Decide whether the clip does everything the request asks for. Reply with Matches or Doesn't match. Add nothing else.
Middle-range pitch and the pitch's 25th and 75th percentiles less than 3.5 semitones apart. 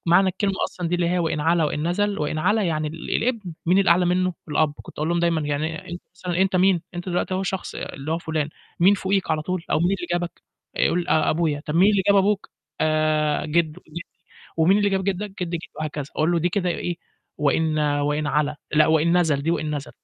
Matches